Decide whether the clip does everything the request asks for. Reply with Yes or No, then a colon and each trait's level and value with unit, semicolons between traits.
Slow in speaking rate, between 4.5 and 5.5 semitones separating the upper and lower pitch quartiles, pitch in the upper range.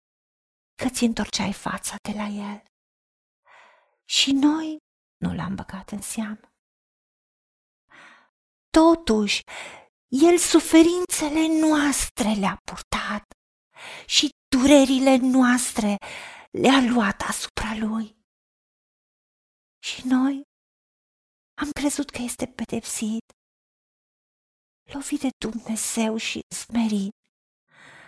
Yes: slow, 85 wpm; average, 5.0 semitones; very high, 255 Hz